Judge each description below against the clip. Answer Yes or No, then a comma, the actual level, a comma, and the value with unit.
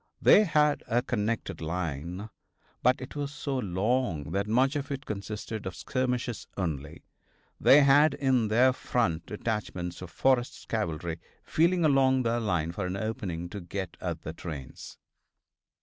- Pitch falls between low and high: No, low, 110 Hz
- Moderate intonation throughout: No, wide, 6.9 semitones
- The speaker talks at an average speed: Yes, average, 150 wpm